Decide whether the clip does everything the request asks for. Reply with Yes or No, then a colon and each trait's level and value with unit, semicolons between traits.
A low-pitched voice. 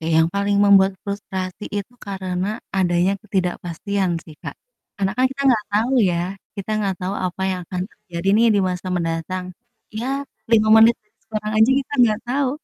No: high, 195 Hz